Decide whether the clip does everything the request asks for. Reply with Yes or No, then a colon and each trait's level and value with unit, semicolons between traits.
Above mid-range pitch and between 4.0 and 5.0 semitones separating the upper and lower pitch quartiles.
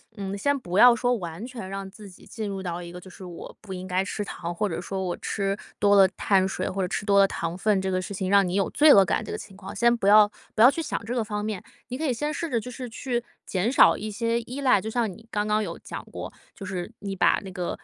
No: high, 200 Hz; average, 3.4 semitones